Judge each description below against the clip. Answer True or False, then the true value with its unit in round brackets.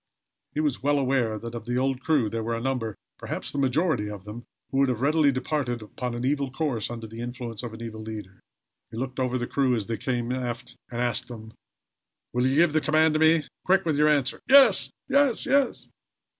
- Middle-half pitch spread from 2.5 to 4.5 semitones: True (3.8 semitones)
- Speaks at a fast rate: True (215 wpm)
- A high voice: False (125 Hz)